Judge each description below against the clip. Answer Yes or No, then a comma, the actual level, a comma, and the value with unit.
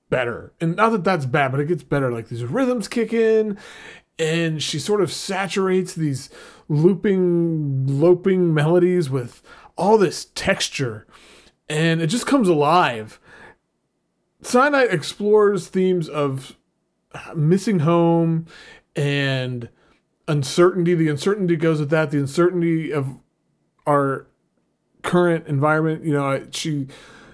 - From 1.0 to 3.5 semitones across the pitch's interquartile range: No, average, 4.2 semitones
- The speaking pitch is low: No, medium, 165 Hz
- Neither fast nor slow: No, slow, 120 wpm